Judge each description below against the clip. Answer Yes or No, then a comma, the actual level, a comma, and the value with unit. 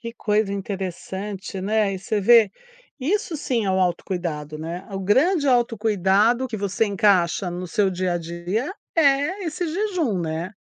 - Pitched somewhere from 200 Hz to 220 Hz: Yes, high, 205 Hz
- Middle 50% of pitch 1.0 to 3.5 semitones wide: No, average, 4.7 semitones